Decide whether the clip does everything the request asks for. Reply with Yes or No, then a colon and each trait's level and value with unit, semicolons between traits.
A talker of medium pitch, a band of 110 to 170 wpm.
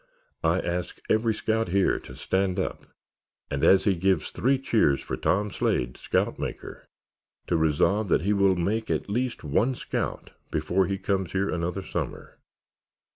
No: very low, 95 Hz; average, 160 wpm